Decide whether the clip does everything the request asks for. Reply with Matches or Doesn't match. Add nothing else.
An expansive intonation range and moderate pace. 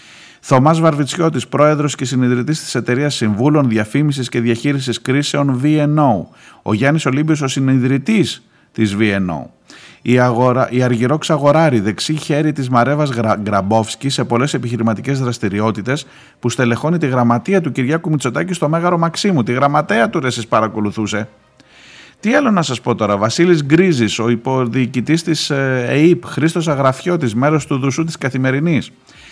Doesn't match